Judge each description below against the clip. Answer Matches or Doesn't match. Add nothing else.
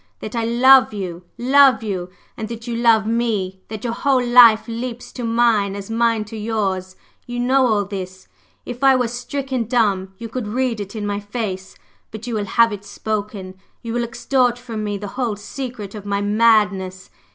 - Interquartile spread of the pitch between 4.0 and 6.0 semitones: Doesn't match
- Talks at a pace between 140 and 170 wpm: Doesn't match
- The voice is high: Matches